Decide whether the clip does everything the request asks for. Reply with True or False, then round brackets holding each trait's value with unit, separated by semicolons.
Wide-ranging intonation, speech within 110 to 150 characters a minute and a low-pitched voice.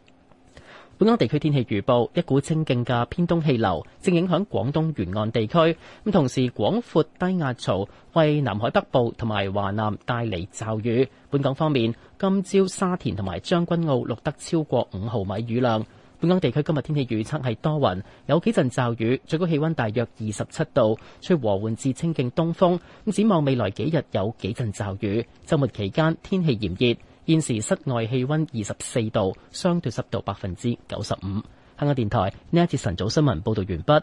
False (6.3 semitones; 285 characters per minute; 125 Hz)